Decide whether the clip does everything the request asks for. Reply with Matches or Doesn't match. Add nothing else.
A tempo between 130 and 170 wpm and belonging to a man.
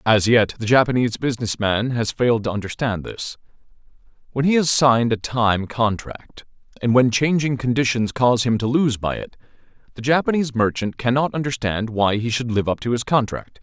Doesn't match